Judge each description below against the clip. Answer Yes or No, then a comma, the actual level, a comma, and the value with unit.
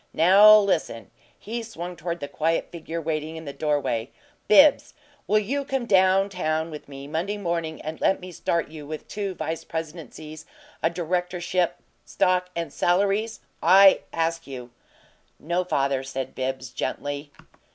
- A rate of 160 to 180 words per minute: No, average, 150 wpm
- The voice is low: No, medium, 165 Hz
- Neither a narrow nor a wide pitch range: Yes, average, 3.6 semitones